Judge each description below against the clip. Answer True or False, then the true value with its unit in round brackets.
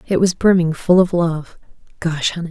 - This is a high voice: False (170 Hz)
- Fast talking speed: False (170 wpm)